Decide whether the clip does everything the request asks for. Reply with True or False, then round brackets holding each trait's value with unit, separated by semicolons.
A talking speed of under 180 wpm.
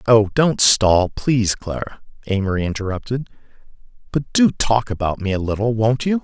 True (155 wpm)